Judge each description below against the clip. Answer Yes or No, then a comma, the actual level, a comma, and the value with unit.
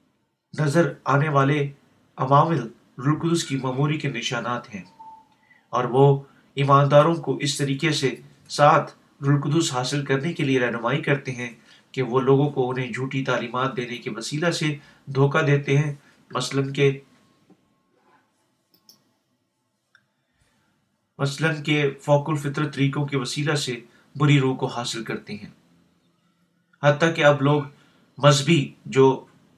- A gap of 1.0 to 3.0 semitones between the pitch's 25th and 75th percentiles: Yes, narrow, 2.4 semitones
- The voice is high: No, medium, 140 Hz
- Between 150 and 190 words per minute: No, average, 125 wpm